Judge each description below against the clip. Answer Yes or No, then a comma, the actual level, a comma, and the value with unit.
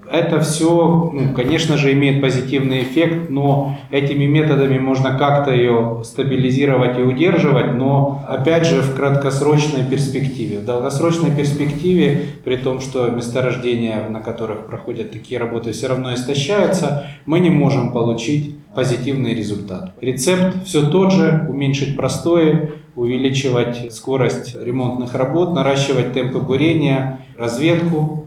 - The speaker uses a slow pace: No, average, 125 wpm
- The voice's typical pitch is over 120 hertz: Yes, low, 135 Hz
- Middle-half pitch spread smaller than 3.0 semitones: No, average, 3.3 semitones